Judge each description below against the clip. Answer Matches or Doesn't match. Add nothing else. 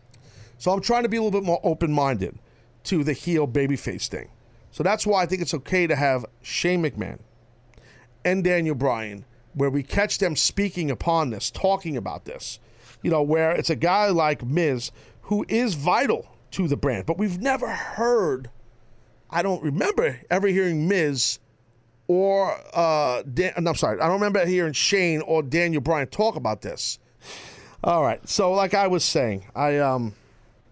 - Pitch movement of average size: Doesn't match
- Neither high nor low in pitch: Matches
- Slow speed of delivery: Doesn't match